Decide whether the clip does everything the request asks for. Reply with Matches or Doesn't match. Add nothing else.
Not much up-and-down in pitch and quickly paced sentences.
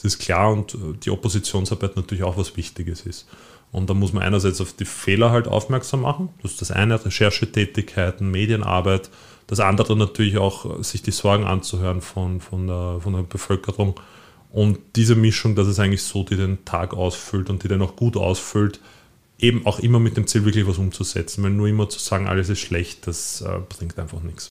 Matches